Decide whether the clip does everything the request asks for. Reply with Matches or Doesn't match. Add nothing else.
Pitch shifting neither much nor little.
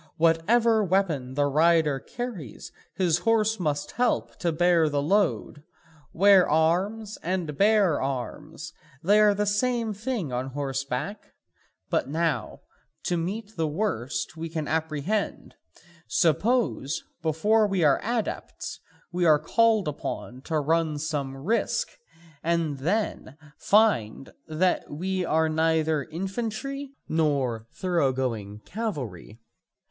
Doesn't match